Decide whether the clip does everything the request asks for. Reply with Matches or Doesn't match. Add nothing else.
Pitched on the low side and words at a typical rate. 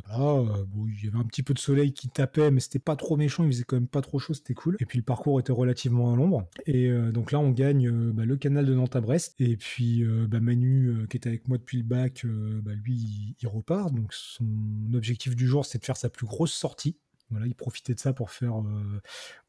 Doesn't match